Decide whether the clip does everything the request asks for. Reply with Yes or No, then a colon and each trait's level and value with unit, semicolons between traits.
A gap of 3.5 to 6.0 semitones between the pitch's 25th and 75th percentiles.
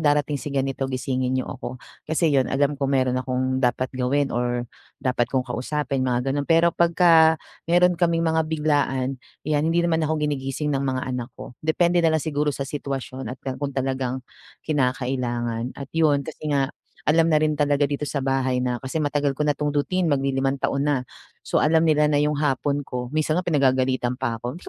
No: average, 2.7 semitones